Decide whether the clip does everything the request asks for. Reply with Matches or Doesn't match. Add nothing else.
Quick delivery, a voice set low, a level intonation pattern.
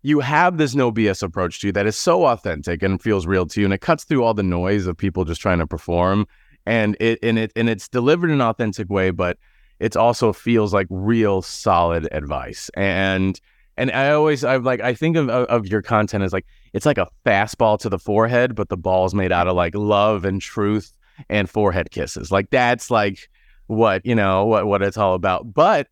Doesn't match